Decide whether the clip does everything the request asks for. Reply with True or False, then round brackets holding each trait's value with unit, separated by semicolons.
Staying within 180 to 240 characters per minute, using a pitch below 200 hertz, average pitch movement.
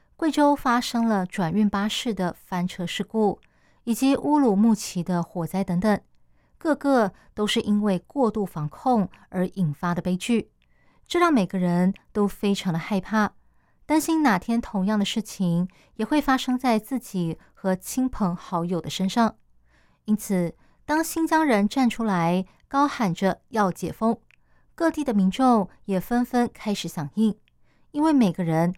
False (225 characters per minute; 210 Hz; 5.0 semitones)